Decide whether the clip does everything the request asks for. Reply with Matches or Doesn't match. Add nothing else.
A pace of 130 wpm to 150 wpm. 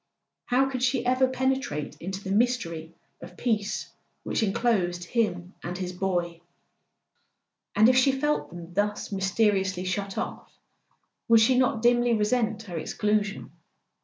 Matches